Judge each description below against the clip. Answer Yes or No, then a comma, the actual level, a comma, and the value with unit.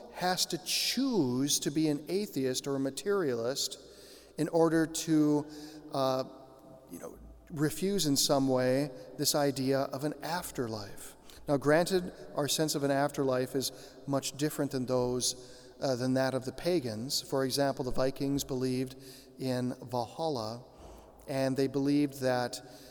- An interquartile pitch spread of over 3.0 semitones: No, average, 2.7 semitones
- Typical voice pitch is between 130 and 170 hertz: Yes, low, 135 Hz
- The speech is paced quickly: No, average, 140 wpm